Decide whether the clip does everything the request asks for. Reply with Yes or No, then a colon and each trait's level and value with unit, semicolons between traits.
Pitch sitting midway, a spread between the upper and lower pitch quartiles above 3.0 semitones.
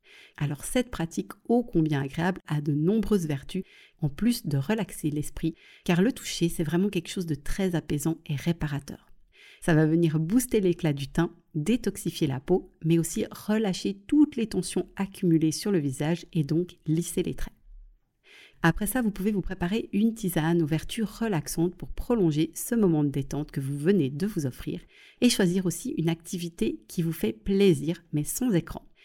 Yes: medium, 170 Hz; average, 4.2 semitones